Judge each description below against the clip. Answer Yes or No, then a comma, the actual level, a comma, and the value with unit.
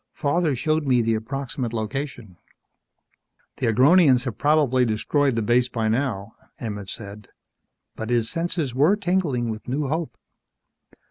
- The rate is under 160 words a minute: Yes, average, 140 wpm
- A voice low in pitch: Yes, low, 125 Hz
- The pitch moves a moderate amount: Yes, average, 4.6 semitones